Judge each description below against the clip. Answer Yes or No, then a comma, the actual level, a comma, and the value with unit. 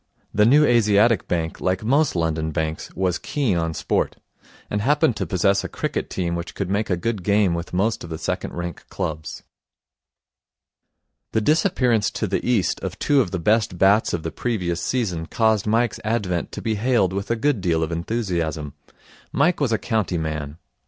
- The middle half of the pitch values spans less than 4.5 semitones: No, average, 5.2 semitones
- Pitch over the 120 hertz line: No, low, 100 Hz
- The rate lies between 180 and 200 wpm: Yes, average, 185 wpm